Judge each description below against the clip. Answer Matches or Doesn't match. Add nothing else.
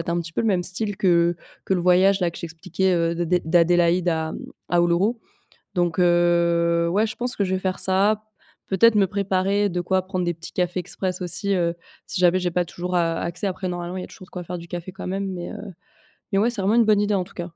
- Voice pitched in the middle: Matches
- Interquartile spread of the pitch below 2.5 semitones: Matches